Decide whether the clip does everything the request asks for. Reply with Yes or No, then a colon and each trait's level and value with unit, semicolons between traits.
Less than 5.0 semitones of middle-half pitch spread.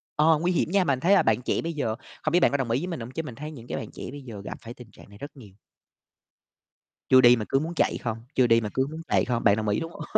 No: average, 5.3 semitones